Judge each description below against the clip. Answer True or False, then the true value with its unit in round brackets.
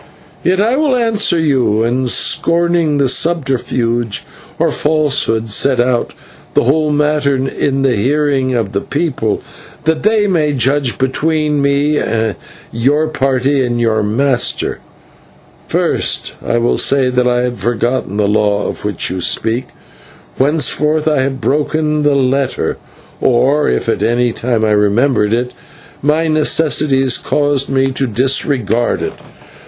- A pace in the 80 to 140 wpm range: True (135 wpm)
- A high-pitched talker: False (135 Hz)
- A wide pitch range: False (3.9 semitones)